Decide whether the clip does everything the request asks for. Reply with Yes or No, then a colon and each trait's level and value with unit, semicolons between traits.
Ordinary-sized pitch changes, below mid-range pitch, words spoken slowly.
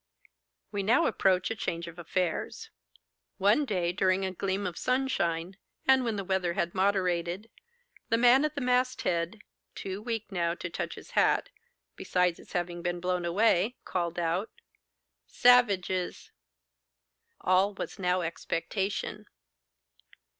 No: average, 3.9 semitones; high, 190 Hz; slow, 125 wpm